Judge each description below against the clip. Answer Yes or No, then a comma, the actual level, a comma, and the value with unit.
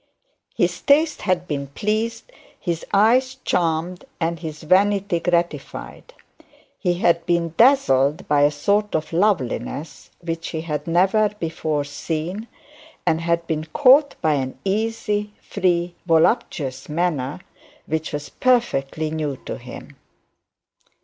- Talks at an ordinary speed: No, slow, 125 wpm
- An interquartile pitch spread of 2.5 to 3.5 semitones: No, average, 4.9 semitones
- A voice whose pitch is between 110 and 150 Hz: No, medium, 170 Hz